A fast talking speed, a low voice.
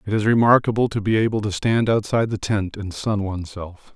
Yes: fast, 210 wpm; low, 105 Hz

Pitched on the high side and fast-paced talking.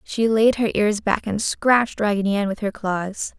Yes: high, 210 Hz; fast, 215 wpm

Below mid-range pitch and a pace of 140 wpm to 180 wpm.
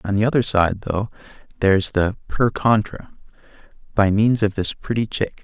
Yes: low, 105 Hz; average, 165 wpm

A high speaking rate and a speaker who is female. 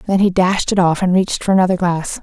Yes: fast, 270 wpm; female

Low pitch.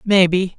No: medium, 185 Hz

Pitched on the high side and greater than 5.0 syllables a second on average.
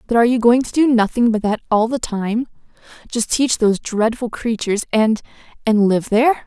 Yes: high, 230 Hz; 5.5 syllables/s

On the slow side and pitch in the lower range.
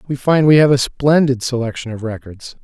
No: fast, 205 wpm; low, 130 Hz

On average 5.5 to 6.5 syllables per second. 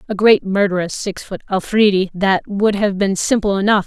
No: 5.0 syllables/s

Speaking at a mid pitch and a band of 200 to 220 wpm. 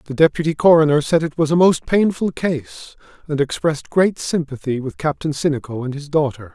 No: medium, 150 Hz; average, 185 wpm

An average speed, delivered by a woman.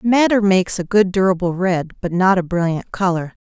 Yes: average, 190 wpm; female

